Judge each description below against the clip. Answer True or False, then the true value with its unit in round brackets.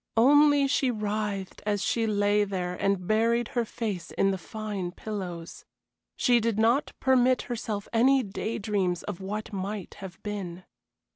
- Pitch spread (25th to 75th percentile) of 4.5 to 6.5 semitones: False (3.1 semitones)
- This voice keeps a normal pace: True (150 wpm)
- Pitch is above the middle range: True (210 Hz)